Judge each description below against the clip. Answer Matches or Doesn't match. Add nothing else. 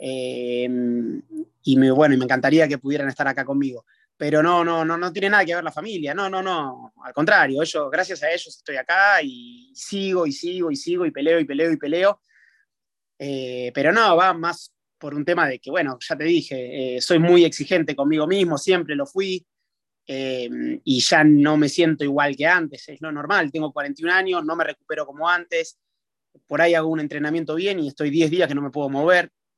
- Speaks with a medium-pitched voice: Matches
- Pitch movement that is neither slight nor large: Matches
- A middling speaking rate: Doesn't match